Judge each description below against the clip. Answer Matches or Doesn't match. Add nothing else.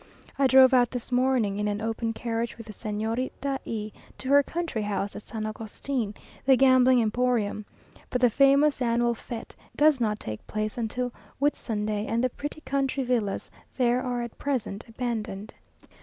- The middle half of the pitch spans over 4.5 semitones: Doesn't match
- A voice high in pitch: Matches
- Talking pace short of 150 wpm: Doesn't match